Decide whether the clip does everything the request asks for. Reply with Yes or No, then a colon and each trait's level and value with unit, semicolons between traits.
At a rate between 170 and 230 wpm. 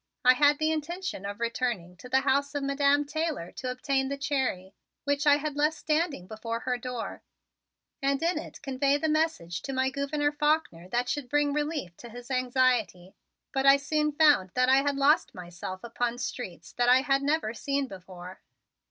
Yes: average, 185 wpm